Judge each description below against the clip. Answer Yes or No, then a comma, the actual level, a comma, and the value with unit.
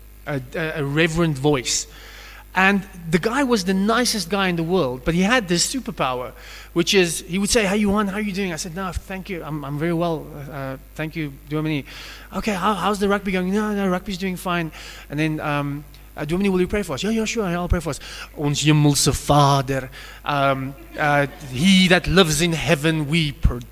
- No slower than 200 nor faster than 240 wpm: Yes, fast, 205 wpm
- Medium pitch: Yes, medium, 170 Hz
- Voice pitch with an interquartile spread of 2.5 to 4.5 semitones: No, average, 4.9 semitones